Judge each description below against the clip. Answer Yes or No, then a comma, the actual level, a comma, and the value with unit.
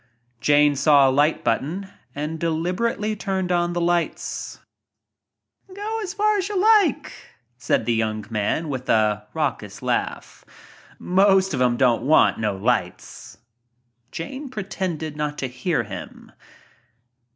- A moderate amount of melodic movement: No, wide, 7.5 semitones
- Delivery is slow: Yes, slow, 130 wpm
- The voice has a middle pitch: Yes, medium, 160 Hz